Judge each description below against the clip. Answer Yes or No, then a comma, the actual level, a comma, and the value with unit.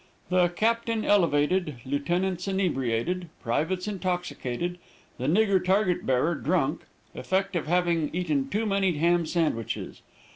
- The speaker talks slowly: Yes, slow, 115 wpm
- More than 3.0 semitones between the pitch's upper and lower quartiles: Yes, average, 3.9 semitones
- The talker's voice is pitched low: No, medium, 175 Hz